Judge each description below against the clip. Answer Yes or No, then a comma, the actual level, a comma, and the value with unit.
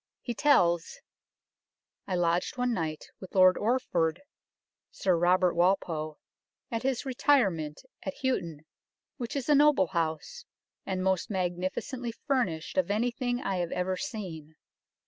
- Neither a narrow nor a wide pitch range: No, wide, 6.3 semitones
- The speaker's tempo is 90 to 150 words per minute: Yes, slow, 135 wpm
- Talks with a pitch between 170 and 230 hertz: Yes, high, 190 Hz